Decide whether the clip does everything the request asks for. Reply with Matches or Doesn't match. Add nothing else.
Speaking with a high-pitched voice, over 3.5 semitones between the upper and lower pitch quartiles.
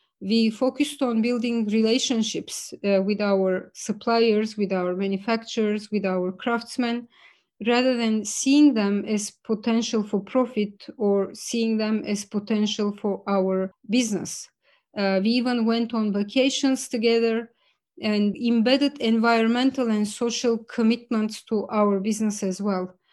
Doesn't match